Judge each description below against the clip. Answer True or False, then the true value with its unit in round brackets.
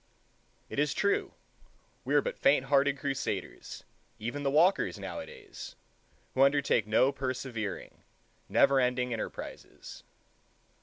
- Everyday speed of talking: False (110 wpm)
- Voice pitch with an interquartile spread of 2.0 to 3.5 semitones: True (2.7 semitones)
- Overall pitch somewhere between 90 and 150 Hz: True (135 Hz)